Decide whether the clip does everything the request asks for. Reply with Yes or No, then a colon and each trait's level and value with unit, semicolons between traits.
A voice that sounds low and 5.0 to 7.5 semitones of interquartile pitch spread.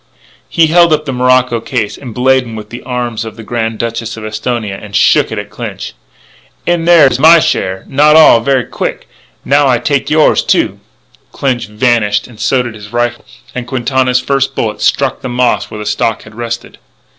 No: low, 120 Hz; average, 3.2 semitones